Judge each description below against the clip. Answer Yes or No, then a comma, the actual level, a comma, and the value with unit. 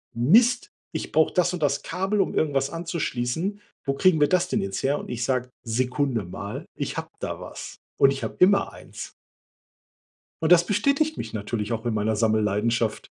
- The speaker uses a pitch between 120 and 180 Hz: Yes, medium, 140 Hz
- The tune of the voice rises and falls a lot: Yes, wide, 7.4 semitones